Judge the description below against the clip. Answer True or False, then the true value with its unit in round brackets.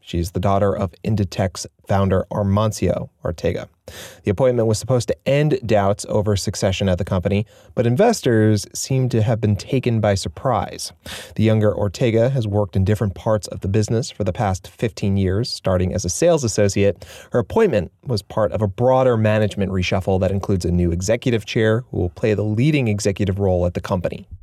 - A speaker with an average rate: True (185 wpm)